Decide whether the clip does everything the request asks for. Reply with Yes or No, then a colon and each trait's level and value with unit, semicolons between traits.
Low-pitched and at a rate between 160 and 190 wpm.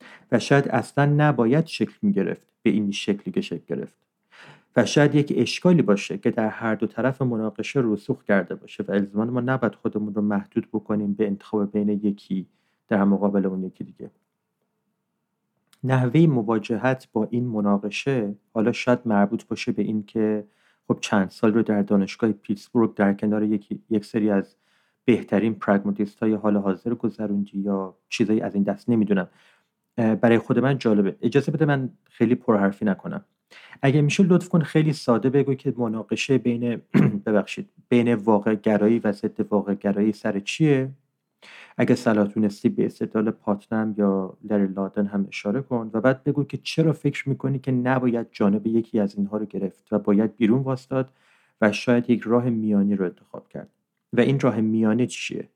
Yes: low, 110 Hz; average, 165 wpm